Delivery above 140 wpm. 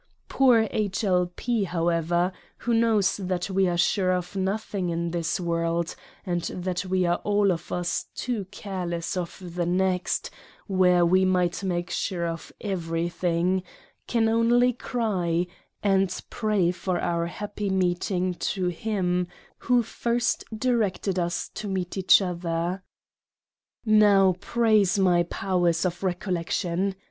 No: slow, 135 wpm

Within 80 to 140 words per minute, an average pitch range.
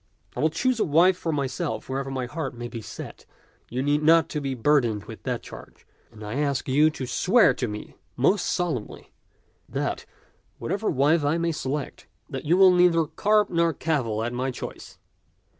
No: average, 185 wpm; average, 4.4 semitones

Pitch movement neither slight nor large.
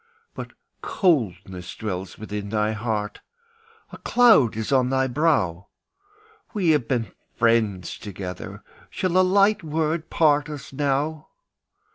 No: wide, 7.2 semitones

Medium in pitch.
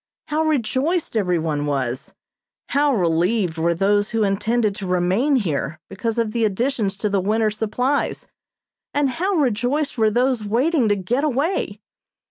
No: high, 220 Hz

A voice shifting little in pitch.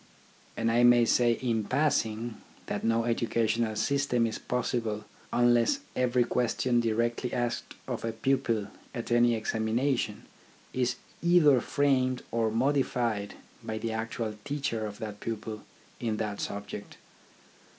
Yes: narrow, 2.0 semitones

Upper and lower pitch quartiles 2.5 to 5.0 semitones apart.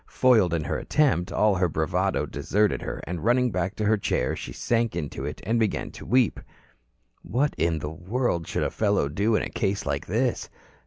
No: wide, 5.5 semitones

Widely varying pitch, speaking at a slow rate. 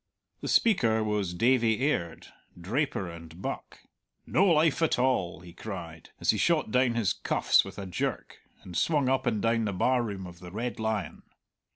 No: wide, 5.9 semitones; average, 180 wpm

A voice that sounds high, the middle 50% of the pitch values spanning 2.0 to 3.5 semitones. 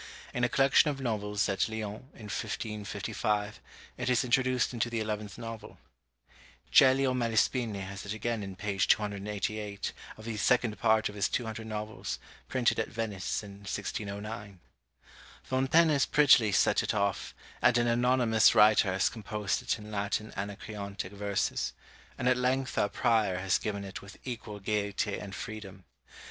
No: low, 105 Hz; average, 2.7 semitones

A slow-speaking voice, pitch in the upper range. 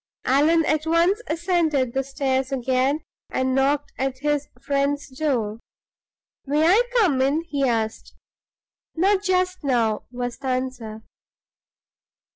Yes: slow, 120 wpm; very high, 275 Hz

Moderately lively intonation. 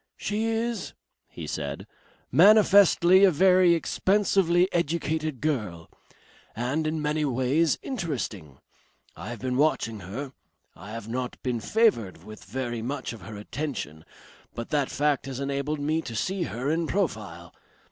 No: wide, 6.7 semitones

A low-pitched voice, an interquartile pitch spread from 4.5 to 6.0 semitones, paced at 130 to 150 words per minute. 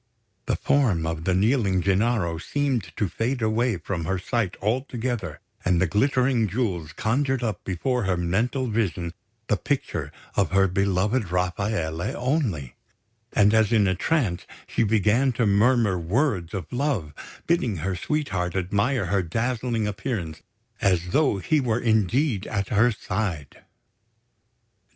Yes: low, 105 Hz; average, 5.2 semitones; average, 140 wpm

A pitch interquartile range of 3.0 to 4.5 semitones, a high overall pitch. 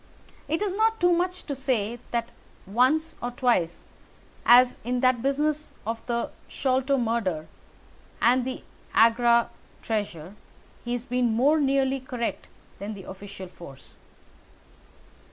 Yes: average, 3.4 semitones; high, 245 Hz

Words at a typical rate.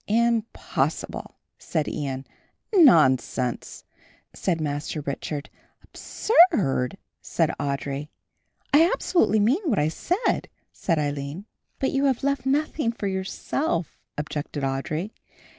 No: slow, 105 wpm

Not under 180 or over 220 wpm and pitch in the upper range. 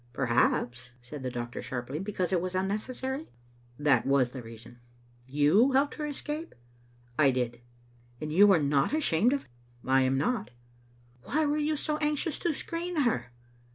No: average, 185 wpm; medium, 150 Hz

